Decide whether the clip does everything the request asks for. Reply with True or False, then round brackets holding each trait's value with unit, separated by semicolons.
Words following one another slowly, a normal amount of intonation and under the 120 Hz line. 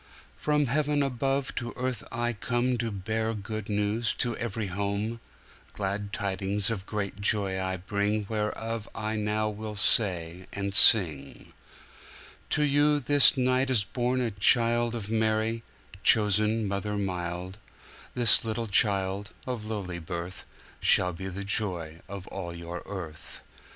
True (120 wpm; 3.1 semitones; 105 Hz)